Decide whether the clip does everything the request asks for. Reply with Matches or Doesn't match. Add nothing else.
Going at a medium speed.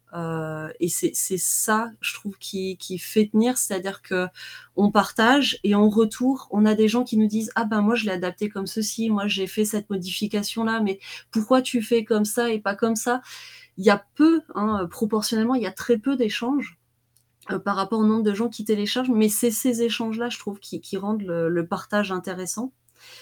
Matches